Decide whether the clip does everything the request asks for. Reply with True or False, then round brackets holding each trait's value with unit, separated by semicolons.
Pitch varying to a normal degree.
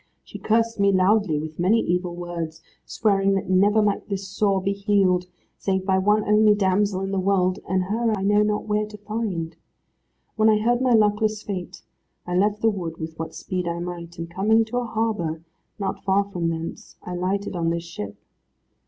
True (3.0 semitones)